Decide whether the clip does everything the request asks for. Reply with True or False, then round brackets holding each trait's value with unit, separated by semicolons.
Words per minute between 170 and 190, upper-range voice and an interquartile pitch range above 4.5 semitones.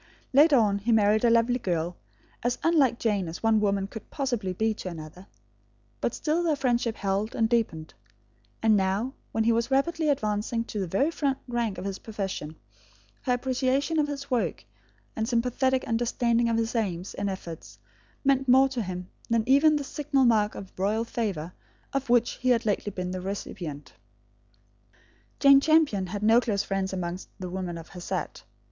True (180 wpm; 225 Hz; 4.9 semitones)